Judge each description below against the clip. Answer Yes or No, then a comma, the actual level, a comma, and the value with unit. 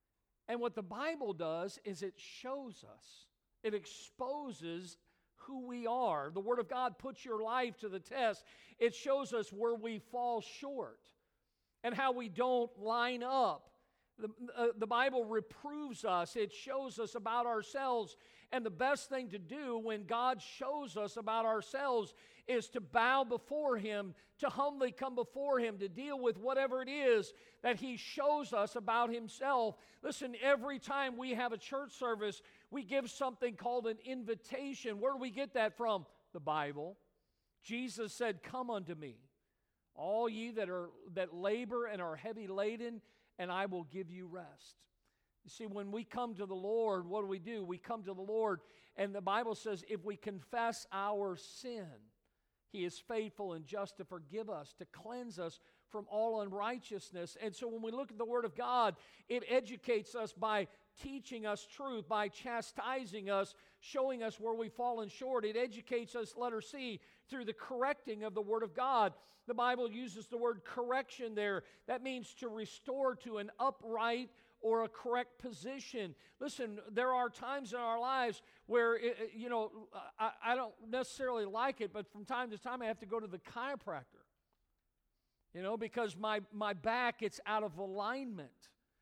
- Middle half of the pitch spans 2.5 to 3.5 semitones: Yes, average, 3.1 semitones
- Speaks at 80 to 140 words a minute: No, average, 175 wpm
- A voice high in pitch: Yes, high, 230 Hz